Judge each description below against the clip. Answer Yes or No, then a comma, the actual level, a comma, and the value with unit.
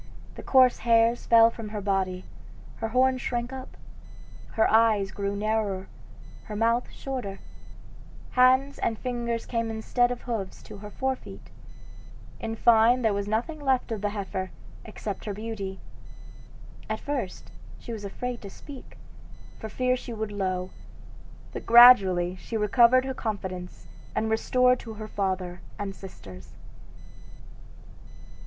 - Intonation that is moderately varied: Yes, average, 3.5 semitones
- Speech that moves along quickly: No, average, 140 wpm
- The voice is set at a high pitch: Yes, high, 220 Hz